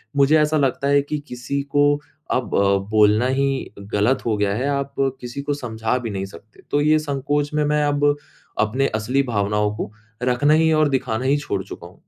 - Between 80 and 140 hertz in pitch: Yes, low, 135 Hz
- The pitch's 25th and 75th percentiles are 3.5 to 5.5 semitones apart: Yes, average, 4.9 semitones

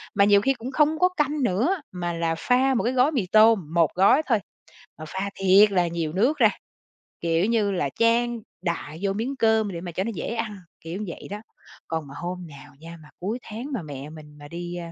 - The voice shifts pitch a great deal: Yes, wide, 5.8 semitones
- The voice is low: No, high, 195 Hz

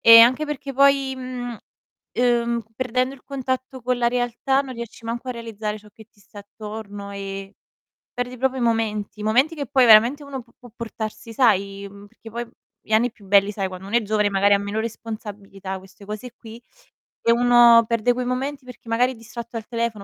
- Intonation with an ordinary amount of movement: Yes, average, 3.0 semitones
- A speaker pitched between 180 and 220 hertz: No, high, 230 Hz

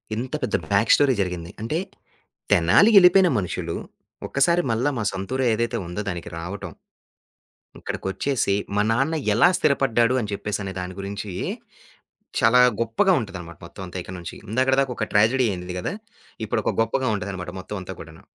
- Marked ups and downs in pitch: Yes, wide, 5.9 semitones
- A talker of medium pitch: No, low, 105 Hz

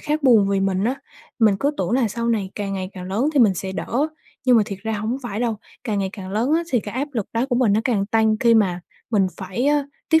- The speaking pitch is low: No, high, 220 Hz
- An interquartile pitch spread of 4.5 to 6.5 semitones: No, average, 3.9 semitones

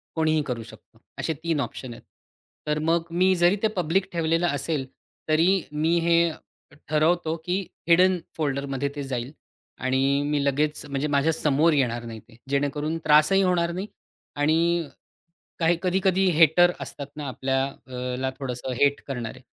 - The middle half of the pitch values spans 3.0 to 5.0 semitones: Yes, average, 3.8 semitones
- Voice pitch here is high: No, medium, 150 Hz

